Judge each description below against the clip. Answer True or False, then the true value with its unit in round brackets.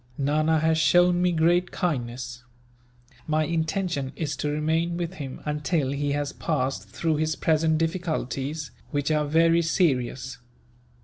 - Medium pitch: True (155 Hz)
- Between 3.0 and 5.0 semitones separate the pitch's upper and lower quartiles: False (2.6 semitones)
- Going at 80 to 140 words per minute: True (135 wpm)